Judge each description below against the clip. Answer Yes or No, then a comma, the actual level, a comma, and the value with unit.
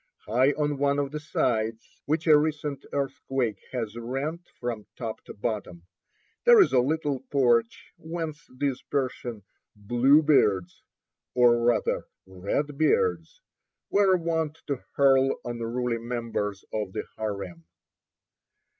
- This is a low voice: Yes, low, 130 Hz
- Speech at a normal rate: No, slow, 120 wpm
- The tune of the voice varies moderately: Yes, average, 4.5 semitones